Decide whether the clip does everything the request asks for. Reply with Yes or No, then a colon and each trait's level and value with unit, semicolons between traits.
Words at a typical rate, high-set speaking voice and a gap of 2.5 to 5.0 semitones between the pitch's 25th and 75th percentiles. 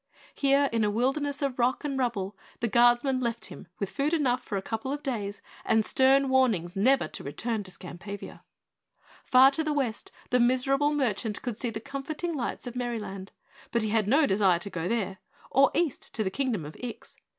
Yes: average, 195 wpm; high, 240 Hz; average, 4.7 semitones